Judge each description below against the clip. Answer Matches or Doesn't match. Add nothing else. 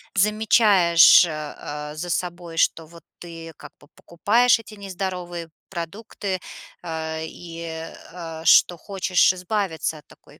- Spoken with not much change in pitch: Doesn't match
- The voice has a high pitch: Doesn't match